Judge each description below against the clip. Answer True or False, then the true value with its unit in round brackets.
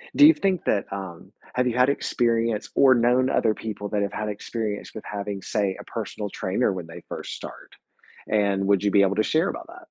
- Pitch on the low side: True (105 Hz)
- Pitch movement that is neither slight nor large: True (3.9 semitones)